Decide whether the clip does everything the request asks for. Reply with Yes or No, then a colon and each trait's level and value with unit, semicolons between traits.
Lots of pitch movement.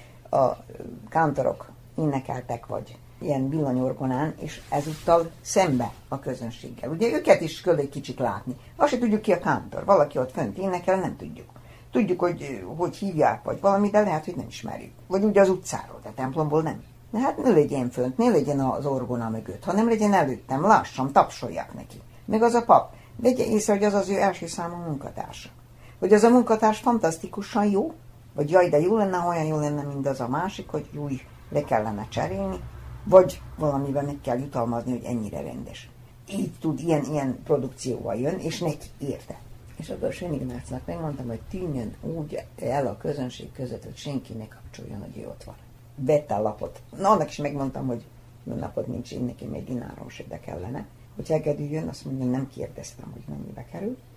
Yes: wide, 6.6 semitones